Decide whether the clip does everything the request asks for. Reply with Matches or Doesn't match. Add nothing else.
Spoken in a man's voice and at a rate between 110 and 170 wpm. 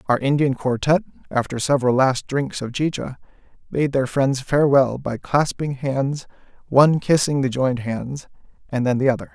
Matches